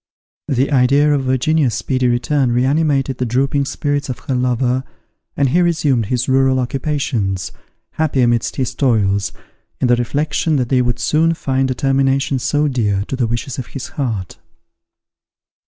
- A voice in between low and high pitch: No, low, 130 Hz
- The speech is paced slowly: No, average, 155 wpm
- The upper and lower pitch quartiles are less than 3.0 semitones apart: Yes, narrow, 2.6 semitones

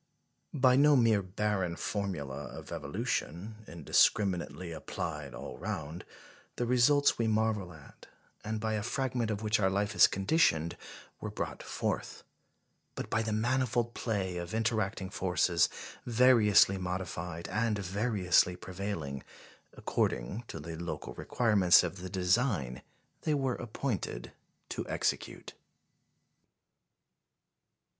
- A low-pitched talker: Yes, low, 100 Hz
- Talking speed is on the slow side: Yes, slow, 120 wpm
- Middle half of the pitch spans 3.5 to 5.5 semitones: Yes, average, 4.2 semitones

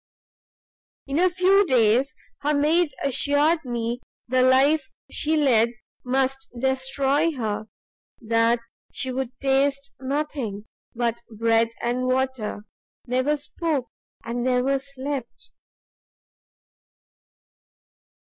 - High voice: Yes, very high, 265 Hz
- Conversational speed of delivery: No, slow, 95 wpm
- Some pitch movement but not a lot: Yes, average, 3.1 semitones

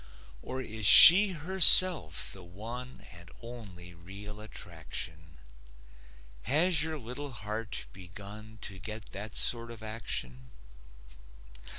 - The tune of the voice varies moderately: No, wide, 5.8 semitones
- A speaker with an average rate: No, slow, 105 wpm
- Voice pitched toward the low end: Yes, low, 110 Hz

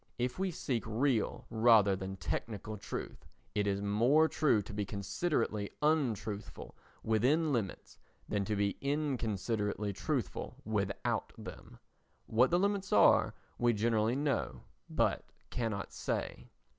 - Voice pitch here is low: Yes, low, 110 Hz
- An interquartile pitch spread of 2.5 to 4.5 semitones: No, average, 5.2 semitones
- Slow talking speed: Yes, slow, 125 wpm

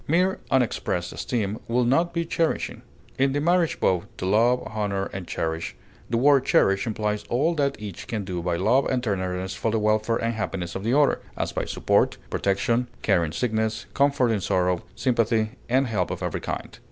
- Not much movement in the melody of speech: No, average, 5.1 semitones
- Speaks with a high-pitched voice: No, low, 110 Hz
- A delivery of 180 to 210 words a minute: Yes, average, 190 wpm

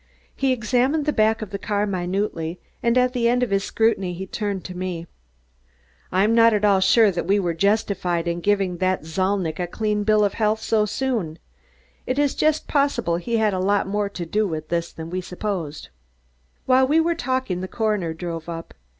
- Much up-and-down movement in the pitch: No, average, 4.3 semitones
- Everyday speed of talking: Yes, average, 195 wpm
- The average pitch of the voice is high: Yes, high, 200 Hz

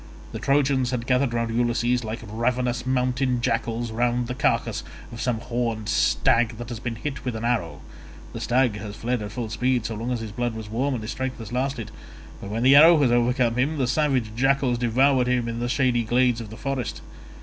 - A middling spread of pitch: No, narrow, 1.9 semitones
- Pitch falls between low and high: No, low, 120 Hz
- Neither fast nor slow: No, fast, 210 wpm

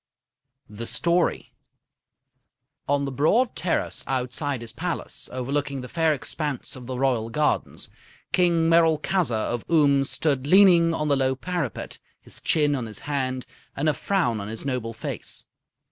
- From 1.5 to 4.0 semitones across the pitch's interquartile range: No, average, 4.4 semitones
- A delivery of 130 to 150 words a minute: Yes, average, 145 wpm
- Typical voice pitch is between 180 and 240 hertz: No, medium, 140 Hz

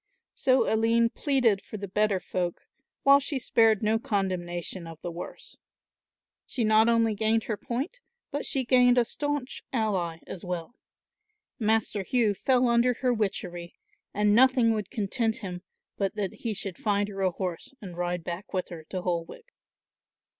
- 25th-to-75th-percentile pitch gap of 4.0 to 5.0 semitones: Yes, average, 4.3 semitones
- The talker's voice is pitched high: Yes, high, 215 Hz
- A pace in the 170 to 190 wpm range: No, average, 160 wpm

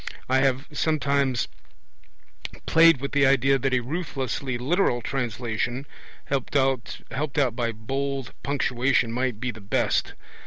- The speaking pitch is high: No, low, 130 Hz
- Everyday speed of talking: No, slow, 120 wpm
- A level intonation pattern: Yes, narrow, 2.3 semitones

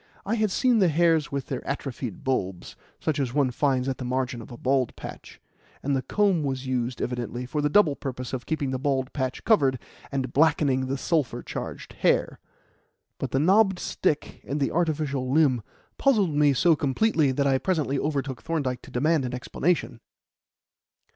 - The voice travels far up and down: No, average, 3.5 semitones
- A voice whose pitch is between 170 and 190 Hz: No, medium, 140 Hz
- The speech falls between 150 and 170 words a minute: No, average, 180 wpm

